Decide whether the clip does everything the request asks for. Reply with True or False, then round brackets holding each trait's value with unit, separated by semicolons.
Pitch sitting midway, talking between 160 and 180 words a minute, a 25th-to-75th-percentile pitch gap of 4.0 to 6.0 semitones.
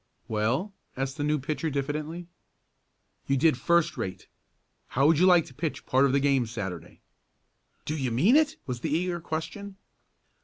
True (145 Hz; 165 wpm; 4.4 semitones)